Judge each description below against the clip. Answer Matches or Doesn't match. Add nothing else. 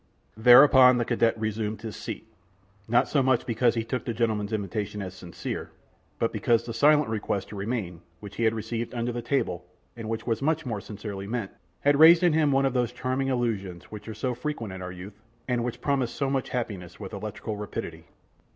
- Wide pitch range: Doesn't match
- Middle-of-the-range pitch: Doesn't match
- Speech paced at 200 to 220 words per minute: Matches